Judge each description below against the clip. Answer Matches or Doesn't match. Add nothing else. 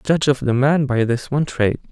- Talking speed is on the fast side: Matches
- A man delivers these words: Matches